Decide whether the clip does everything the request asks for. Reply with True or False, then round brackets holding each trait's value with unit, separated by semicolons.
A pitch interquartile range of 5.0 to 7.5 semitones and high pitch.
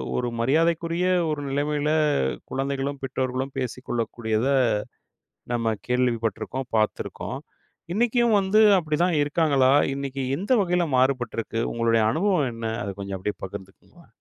False (5.4 semitones; 135 Hz)